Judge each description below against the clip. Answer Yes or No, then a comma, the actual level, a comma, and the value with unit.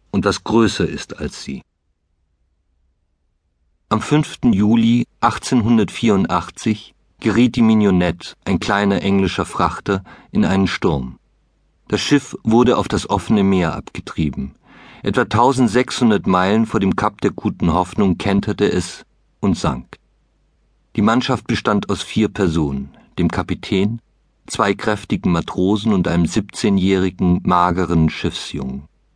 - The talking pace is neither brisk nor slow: No, slow, 115 wpm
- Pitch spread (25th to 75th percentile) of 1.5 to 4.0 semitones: No, average, 4.8 semitones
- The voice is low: Yes, low, 100 Hz